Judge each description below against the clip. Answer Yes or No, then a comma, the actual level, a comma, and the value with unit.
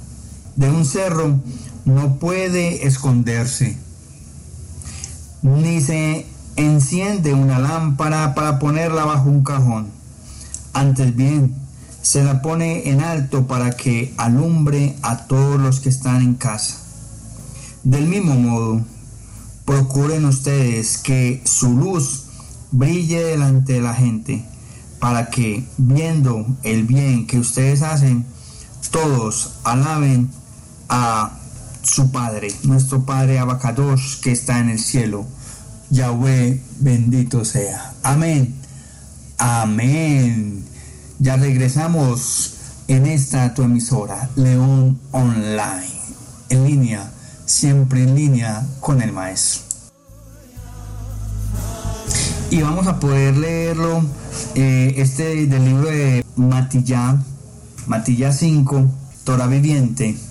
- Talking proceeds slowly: Yes, slow, 100 wpm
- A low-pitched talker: Yes, low, 130 Hz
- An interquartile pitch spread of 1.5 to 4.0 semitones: Yes, average, 2.7 semitones